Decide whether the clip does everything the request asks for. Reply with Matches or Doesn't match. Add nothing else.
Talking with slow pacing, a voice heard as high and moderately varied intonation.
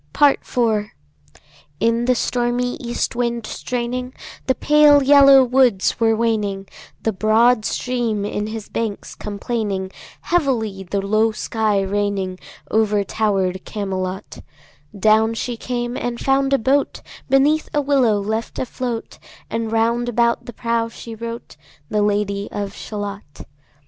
Matches